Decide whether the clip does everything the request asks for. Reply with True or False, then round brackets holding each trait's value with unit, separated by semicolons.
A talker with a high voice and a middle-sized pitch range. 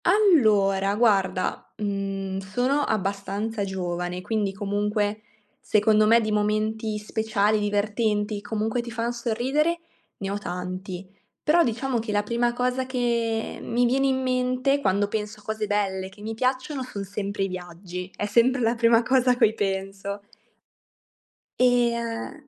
True (215 Hz; 3.2 semitones)